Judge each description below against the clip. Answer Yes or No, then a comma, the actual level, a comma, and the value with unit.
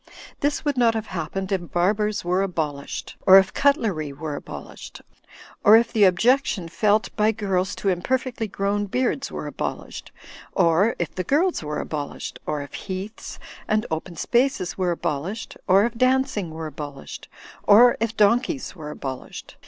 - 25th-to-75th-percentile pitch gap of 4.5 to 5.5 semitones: Yes, average, 5.1 semitones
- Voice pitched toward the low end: No, high, 195 Hz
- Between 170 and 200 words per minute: No, average, 155 wpm